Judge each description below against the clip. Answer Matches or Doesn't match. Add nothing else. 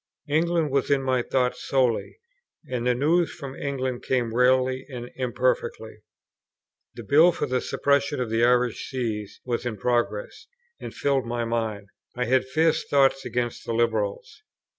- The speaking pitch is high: Doesn't match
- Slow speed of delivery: Doesn't match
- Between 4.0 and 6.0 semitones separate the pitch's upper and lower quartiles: Doesn't match